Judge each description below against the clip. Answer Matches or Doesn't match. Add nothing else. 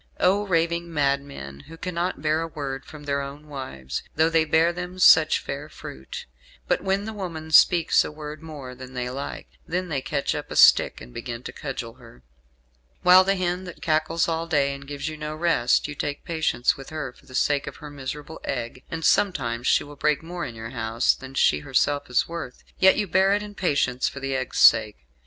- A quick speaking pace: Matches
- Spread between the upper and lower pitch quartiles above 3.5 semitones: Matches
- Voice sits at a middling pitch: Matches